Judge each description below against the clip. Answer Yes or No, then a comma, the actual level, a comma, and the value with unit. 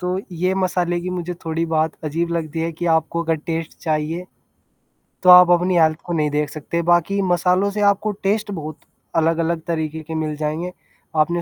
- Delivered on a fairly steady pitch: Yes, narrow, 2.2 semitones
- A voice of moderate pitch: Yes, medium, 170 Hz